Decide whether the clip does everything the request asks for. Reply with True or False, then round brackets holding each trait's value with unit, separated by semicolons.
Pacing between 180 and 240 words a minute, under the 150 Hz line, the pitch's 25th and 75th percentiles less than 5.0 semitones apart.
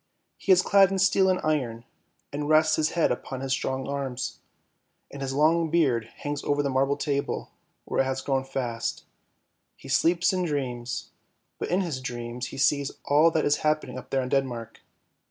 True (185 wpm; 140 Hz; 3.1 semitones)